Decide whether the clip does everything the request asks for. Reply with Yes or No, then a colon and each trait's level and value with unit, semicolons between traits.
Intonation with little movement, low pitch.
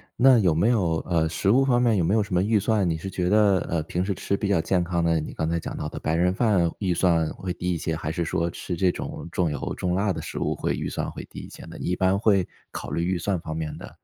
No: average, 3.0 semitones; very low, 90 Hz